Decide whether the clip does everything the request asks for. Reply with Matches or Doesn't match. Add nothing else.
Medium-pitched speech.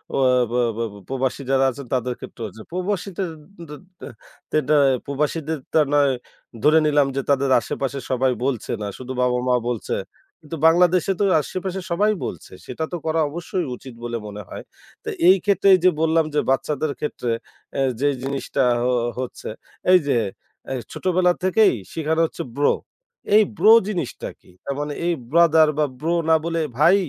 Matches